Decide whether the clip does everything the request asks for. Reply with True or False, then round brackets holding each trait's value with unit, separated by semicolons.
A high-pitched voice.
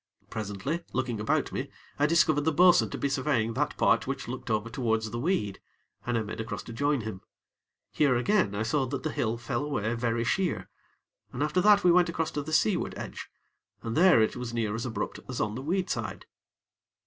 False (125 Hz)